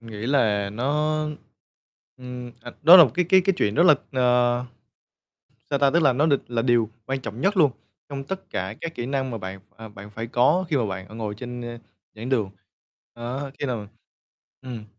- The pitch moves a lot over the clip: No, average, 3.9 semitones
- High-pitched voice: No, low, 125 Hz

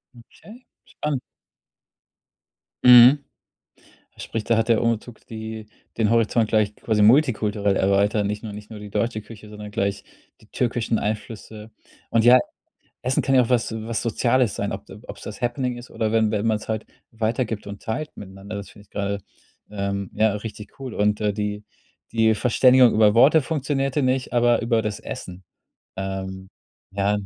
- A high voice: No, low, 110 Hz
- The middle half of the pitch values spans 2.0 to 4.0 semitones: Yes, narrow, 2.6 semitones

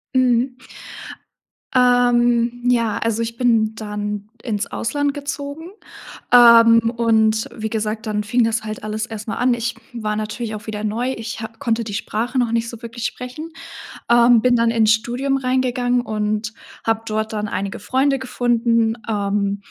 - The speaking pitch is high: Yes, high, 230 Hz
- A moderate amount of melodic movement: No, narrow, 2.2 semitones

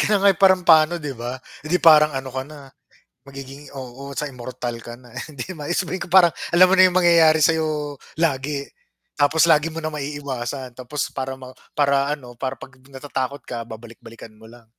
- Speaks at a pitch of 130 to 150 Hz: Yes, medium, 140 Hz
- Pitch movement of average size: Yes, average, 3.8 semitones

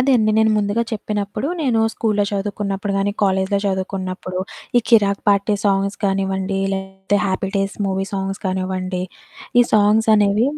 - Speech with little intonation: Yes, narrow, 1.4 semitones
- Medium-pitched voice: No, high, 200 Hz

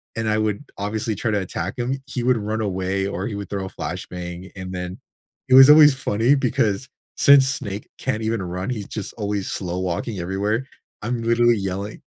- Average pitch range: Yes, average, 3.8 semitones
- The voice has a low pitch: Yes, low, 105 Hz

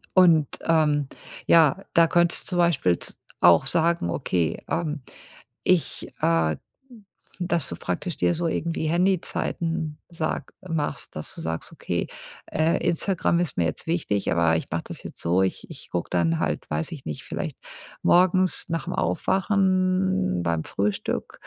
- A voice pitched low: No, medium, 155 Hz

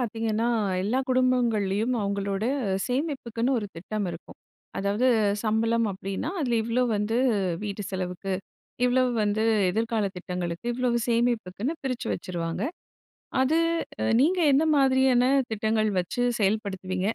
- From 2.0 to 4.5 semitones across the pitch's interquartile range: Yes, average, 4.0 semitones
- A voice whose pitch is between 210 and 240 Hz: Yes, high, 220 Hz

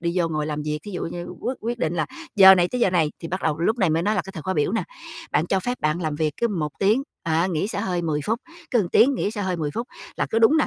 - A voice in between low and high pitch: Yes, medium, 180 Hz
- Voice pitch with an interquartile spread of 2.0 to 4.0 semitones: No, average, 5.2 semitones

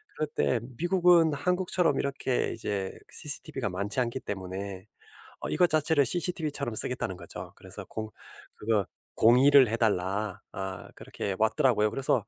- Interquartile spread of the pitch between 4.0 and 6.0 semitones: No, wide, 6.6 semitones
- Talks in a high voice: No, low, 120 Hz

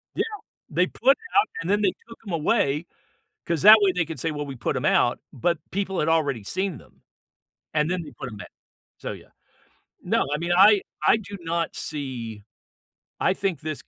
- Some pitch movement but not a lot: Yes, average, 4.7 semitones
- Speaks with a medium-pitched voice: Yes, medium, 170 Hz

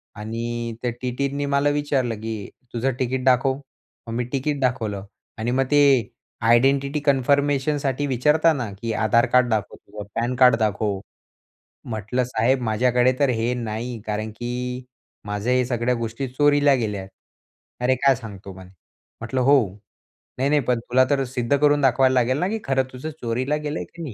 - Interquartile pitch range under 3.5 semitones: Yes, average, 3.1 semitones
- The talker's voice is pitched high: No, low, 125 Hz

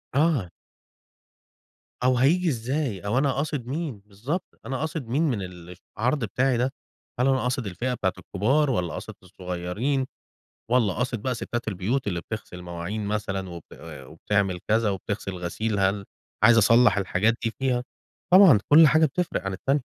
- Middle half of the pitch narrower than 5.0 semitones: No, wide, 5.5 semitones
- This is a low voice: Yes, low, 115 Hz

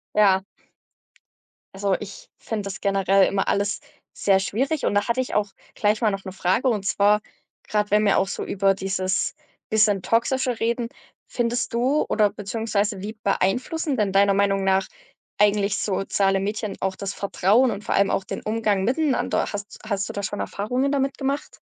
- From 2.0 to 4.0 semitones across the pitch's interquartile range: Yes, average, 2.7 semitones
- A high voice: Yes, high, 205 Hz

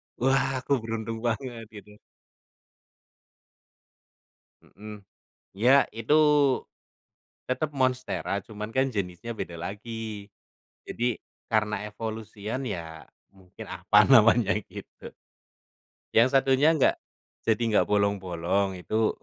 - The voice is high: No, low, 110 Hz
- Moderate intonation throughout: Yes, average, 3.7 semitones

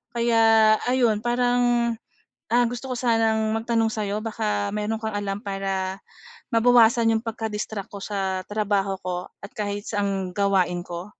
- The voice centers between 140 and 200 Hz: No, high, 215 Hz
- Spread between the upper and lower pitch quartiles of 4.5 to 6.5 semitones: No, narrow, 2.6 semitones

